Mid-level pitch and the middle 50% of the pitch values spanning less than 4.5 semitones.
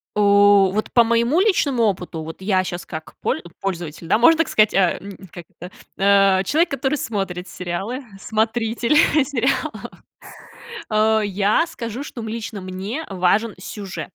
No: high, 205 Hz; average, 3.9 semitones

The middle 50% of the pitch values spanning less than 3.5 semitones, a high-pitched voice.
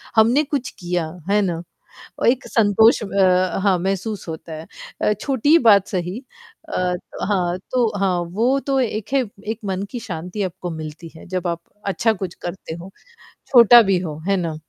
No: average, 4.2 semitones; high, 195 Hz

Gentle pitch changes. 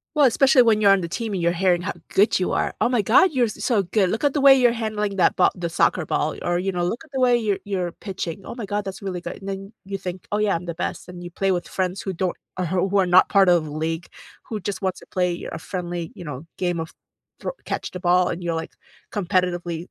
No: average, 3.0 semitones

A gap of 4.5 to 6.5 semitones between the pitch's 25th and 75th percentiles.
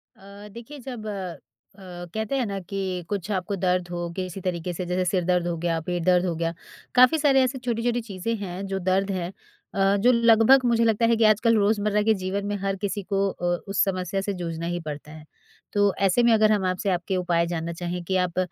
No: average, 3.5 semitones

